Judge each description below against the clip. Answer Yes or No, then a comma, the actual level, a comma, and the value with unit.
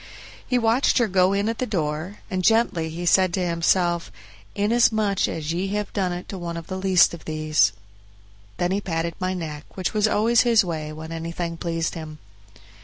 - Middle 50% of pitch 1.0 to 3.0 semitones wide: No, average, 3.7 semitones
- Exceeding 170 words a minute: Yes, average, 190 wpm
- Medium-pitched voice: Yes, medium, 180 Hz